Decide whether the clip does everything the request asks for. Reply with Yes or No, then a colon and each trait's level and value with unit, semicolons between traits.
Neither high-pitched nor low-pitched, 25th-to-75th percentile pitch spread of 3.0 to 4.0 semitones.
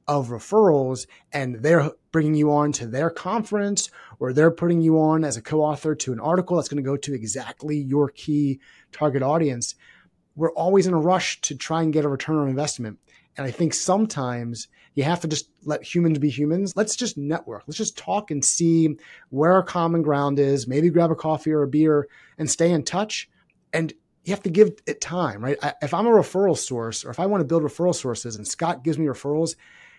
Yes: medium, 155 Hz; average, 3.3 semitones